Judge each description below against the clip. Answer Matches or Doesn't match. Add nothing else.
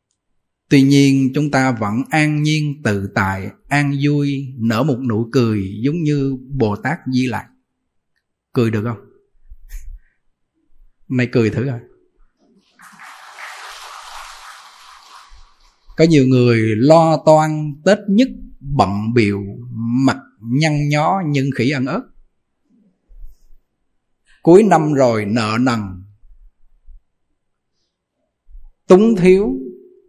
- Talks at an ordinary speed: Doesn't match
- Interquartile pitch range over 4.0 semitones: Matches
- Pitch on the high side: Doesn't match